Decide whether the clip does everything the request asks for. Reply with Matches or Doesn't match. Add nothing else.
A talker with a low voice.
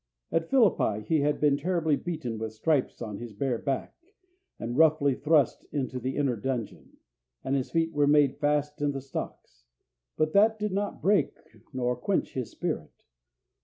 Doesn't match